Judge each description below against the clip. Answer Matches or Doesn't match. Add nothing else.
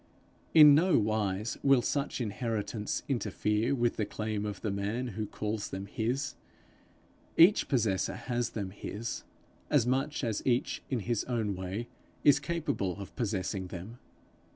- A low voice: Matches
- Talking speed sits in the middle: Matches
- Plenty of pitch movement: Doesn't match